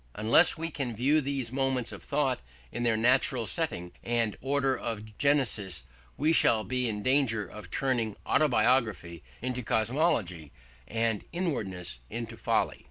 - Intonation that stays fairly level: No, average, 4.0 semitones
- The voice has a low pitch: Yes, low, 120 Hz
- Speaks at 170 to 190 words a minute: No, average, 140 wpm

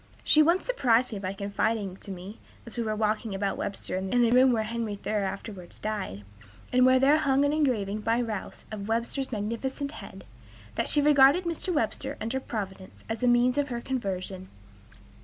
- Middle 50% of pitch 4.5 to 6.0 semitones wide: Yes, average, 4.8 semitones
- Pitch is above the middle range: Yes, high, 230 Hz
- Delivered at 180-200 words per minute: Yes, average, 190 wpm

